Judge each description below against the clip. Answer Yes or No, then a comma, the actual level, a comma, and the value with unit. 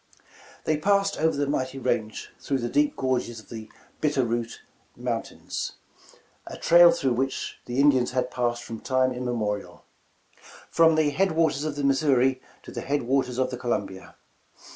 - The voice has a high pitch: No, low, 130 Hz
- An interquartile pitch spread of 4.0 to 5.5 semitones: No, average, 3.3 semitones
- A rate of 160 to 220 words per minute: Yes, average, 165 wpm